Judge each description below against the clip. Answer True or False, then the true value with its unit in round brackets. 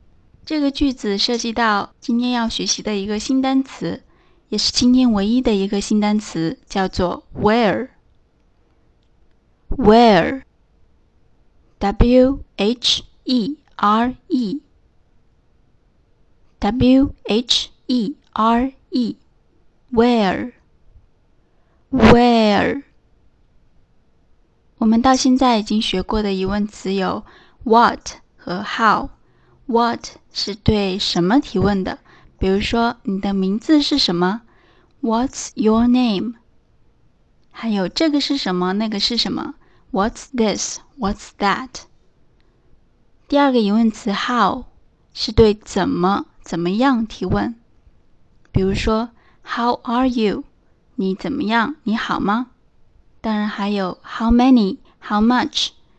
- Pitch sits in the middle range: False (230 Hz)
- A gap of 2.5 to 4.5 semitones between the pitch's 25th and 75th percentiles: True (3.8 semitones)